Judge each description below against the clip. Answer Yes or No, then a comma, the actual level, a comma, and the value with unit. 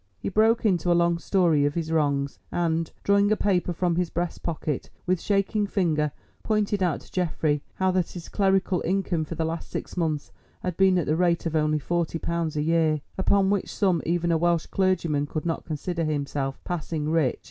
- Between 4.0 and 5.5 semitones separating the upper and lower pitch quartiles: No, average, 3.0 semitones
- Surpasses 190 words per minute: Yes, average, 200 wpm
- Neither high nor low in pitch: Yes, medium, 170 Hz